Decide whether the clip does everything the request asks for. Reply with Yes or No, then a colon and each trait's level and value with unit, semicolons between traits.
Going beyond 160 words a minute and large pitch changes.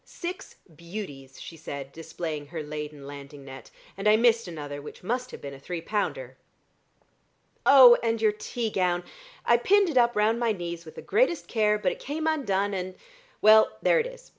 Yes: average, 190 wpm; wide, 7.4 semitones